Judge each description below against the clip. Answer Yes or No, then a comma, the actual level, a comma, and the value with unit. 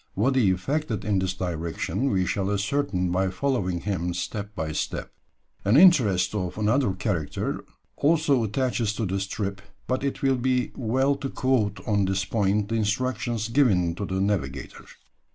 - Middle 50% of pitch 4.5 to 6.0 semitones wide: Yes, average, 5.2 semitones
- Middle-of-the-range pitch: No, low, 105 Hz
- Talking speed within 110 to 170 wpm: Yes, average, 160 wpm